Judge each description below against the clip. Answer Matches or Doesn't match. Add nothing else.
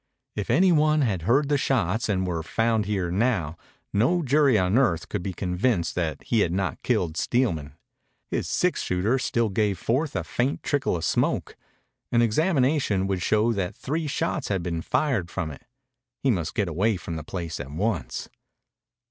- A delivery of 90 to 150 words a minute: Doesn't match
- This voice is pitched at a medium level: Doesn't match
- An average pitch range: Doesn't match